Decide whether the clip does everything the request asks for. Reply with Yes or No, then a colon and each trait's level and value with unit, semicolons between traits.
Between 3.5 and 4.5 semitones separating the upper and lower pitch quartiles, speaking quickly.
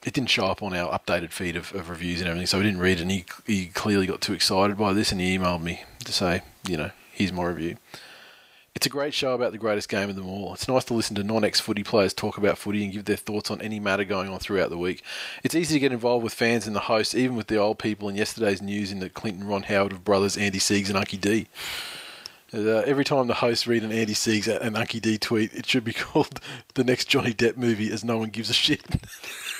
No: average, 3.0 semitones; fast, 265 wpm